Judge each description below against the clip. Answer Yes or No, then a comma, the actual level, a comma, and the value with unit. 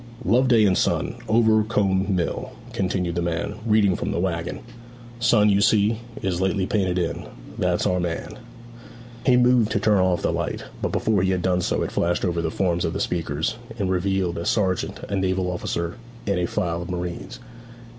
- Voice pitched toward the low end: Yes, very low, 95 Hz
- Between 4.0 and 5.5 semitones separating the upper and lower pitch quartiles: No, average, 3.2 semitones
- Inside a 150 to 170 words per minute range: No, average, 185 wpm